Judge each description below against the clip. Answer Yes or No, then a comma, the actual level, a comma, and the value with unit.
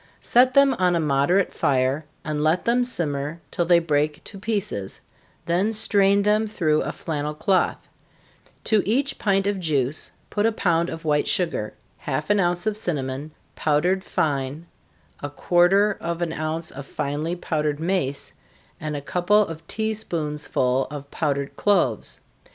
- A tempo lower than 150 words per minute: No, average, 155 wpm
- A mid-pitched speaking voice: Yes, medium, 170 Hz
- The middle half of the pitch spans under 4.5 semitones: No, average, 5.1 semitones